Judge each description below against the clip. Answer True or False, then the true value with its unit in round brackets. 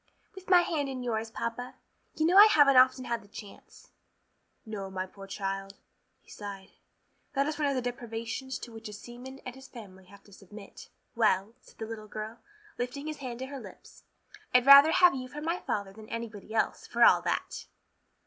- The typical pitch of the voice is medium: False (235 Hz)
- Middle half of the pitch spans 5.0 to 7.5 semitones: False (4.5 semitones)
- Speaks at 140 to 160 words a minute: False (195 wpm)